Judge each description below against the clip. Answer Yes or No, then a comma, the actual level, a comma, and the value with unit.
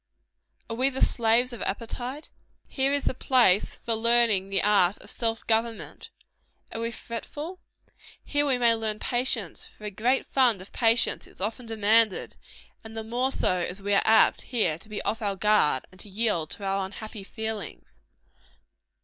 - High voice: Yes, high, 225 Hz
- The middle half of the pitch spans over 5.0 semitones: No, average, 3.0 semitones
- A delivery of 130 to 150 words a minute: No, average, 175 wpm